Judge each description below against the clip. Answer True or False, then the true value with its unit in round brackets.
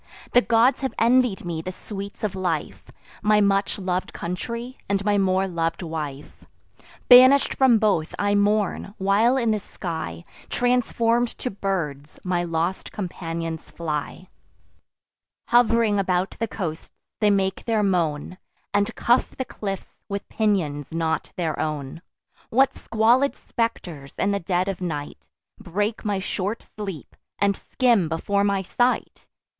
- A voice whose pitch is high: True (195 Hz)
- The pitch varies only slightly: False (4.6 semitones)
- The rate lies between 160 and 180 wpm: False (140 wpm)